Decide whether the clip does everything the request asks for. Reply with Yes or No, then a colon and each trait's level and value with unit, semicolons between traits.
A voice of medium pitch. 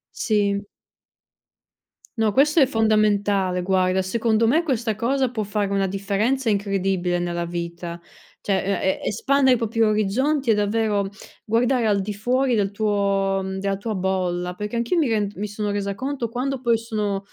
No: high, 210 Hz